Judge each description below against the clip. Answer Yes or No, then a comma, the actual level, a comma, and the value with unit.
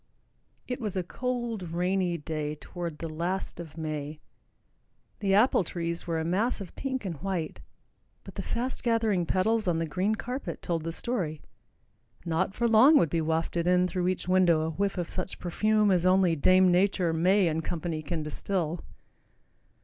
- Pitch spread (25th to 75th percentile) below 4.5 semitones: Yes, average, 3.5 semitones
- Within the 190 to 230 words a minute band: No, average, 170 wpm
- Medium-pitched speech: Yes, medium, 180 Hz